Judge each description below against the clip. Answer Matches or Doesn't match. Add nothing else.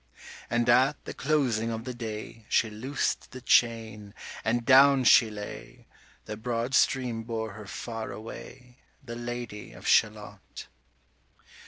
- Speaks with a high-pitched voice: Doesn't match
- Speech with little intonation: Matches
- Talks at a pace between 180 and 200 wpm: Doesn't match